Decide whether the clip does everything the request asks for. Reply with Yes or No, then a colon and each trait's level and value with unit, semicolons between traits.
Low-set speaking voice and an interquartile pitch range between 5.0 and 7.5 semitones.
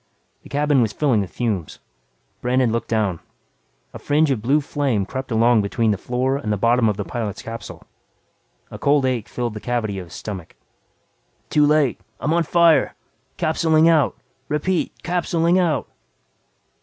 Yes: low, 125 Hz; average, 5.3 semitones